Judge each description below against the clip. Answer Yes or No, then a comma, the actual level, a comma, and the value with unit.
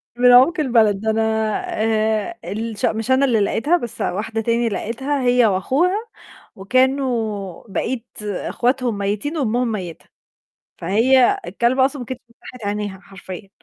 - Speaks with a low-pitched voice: No, high, 230 Hz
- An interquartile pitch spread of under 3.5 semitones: No, average, 3.8 semitones